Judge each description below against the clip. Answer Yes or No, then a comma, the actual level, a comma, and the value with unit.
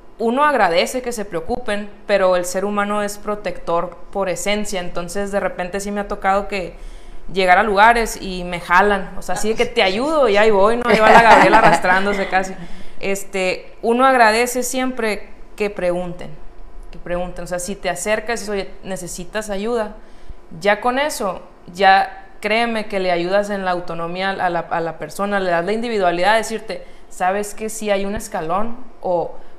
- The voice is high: Yes, high, 200 Hz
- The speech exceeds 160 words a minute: Yes, average, 180 wpm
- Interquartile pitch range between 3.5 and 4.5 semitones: No, average, 3.0 semitones